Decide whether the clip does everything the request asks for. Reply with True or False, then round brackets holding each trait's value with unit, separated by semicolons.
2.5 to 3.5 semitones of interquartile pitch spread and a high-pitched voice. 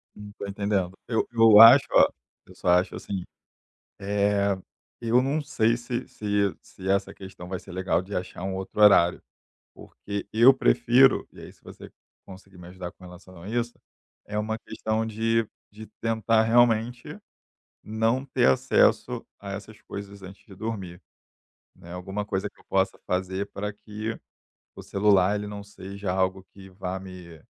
False (2.9 semitones; 100 Hz)